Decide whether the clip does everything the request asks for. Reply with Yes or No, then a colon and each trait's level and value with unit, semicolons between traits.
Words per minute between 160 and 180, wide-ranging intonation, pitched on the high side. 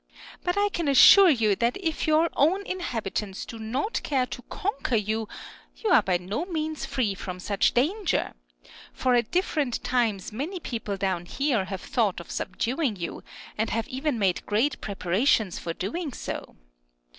Yes: average, 165 wpm; wide, 7.3 semitones; high, 245 Hz